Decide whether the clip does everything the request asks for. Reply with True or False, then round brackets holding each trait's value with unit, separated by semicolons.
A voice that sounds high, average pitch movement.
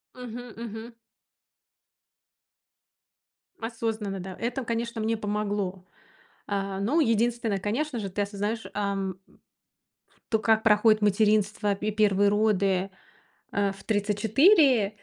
False (210 Hz; 2.2 semitones)